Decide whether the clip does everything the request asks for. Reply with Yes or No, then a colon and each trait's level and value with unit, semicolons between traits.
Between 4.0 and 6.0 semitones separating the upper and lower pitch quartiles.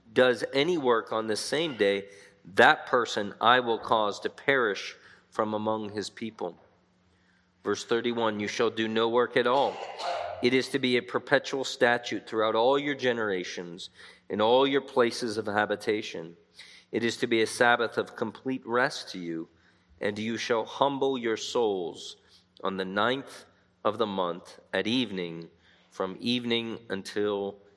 Yes: average, 4.4 semitones